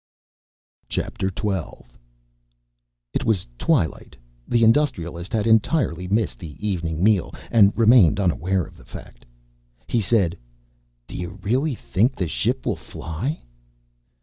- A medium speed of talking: No, slow, 120 wpm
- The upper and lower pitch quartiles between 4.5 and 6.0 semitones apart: Yes, average, 4.8 semitones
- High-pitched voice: No, low, 100 Hz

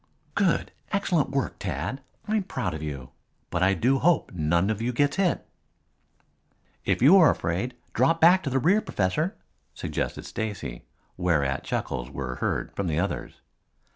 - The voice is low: Yes, low, 110 Hz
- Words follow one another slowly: No, average, 160 wpm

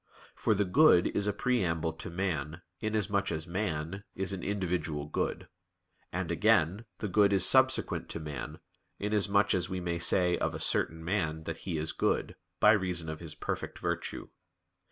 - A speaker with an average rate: Yes, average, 170 wpm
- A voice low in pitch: Yes, very low, 90 Hz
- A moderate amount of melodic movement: Yes, average, 3.6 semitones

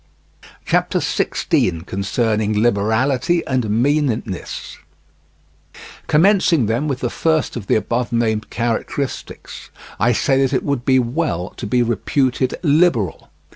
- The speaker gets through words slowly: Yes, slow, 120 wpm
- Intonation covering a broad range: No, average, 4.2 semitones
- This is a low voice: Yes, low, 120 Hz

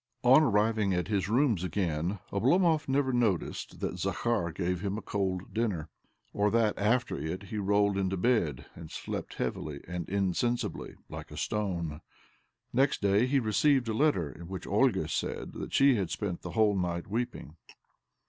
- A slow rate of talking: No, average, 165 wpm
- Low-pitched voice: Yes, low, 100 Hz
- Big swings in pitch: No, average, 4.8 semitones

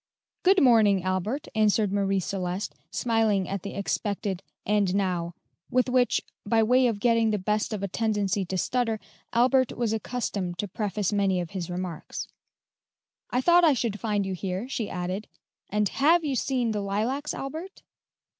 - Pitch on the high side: Yes, high, 210 Hz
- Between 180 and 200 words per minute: No, average, 165 wpm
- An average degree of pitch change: Yes, average, 4.0 semitones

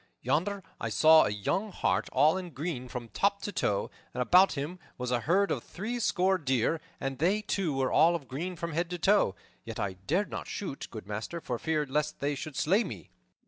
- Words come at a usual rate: No, fast, 210 wpm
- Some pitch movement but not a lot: No, wide, 6.2 semitones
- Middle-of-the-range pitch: Yes, medium, 155 Hz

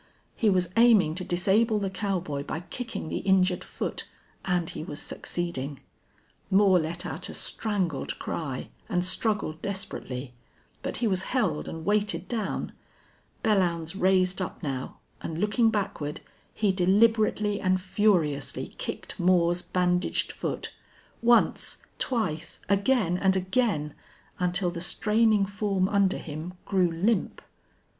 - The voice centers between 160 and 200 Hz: Yes, medium, 185 Hz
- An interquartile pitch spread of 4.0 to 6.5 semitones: No, average, 3.4 semitones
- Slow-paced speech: Yes, slow, 130 wpm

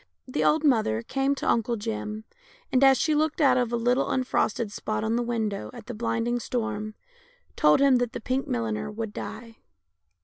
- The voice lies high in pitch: Yes, high, 235 Hz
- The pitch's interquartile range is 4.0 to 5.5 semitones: No, average, 3.0 semitones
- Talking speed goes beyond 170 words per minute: Yes, average, 190 wpm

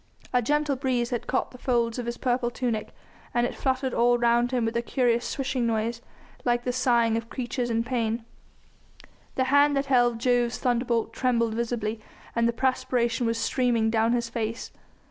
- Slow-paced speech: No, average, 180 wpm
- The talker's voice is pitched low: No, high, 240 Hz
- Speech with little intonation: Yes, narrow, 1.6 semitones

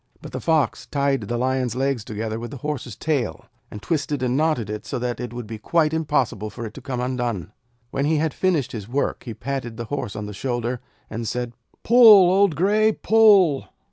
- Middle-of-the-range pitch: No, low, 130 Hz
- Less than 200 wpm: No, fast, 205 wpm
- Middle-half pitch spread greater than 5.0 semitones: No, average, 4.7 semitones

